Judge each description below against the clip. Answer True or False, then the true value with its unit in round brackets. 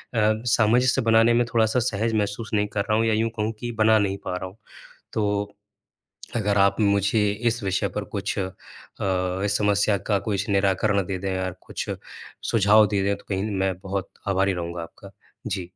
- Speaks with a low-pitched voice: True (105 Hz)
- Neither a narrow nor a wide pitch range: False (2.2 semitones)